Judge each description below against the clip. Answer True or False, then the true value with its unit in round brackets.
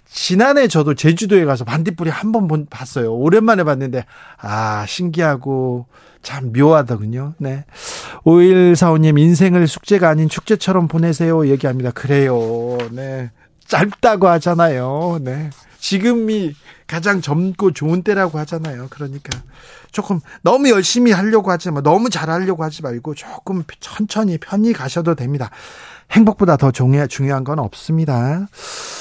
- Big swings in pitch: True (5.7 semitones)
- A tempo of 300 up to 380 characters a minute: True (310 characters per minute)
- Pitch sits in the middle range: True (160 Hz)